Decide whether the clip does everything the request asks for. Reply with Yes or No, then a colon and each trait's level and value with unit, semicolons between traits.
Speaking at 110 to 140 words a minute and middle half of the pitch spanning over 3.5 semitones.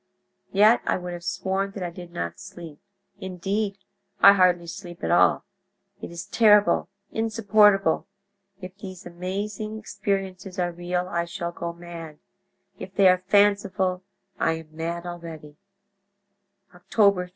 No: slow, 135 wpm; narrow, 2.6 semitones